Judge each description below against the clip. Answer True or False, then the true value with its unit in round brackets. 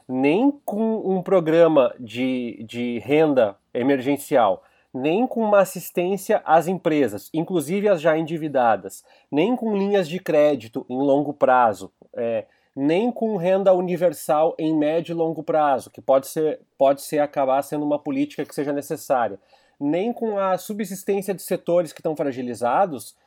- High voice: False (165 Hz)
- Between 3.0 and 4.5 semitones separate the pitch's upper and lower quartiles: False (5.3 semitones)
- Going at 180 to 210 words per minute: False (145 wpm)